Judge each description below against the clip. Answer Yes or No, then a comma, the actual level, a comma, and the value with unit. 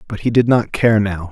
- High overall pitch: No, low, 110 Hz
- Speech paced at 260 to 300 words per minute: Yes, fast, 275 wpm